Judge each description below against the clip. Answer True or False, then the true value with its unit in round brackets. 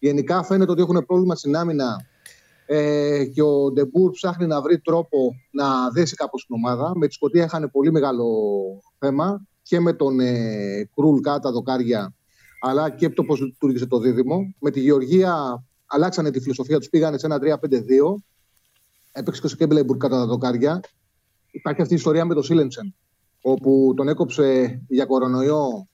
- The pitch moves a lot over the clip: False (4.3 semitones)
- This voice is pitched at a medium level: True (145 Hz)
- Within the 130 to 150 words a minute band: False (165 wpm)